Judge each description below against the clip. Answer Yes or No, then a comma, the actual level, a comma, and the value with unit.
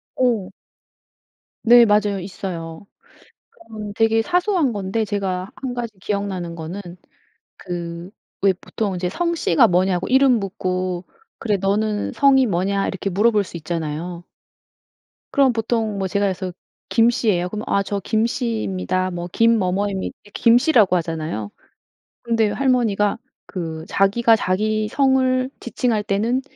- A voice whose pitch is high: Yes, high, 205 Hz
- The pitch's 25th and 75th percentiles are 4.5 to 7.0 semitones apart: No, average, 4.0 semitones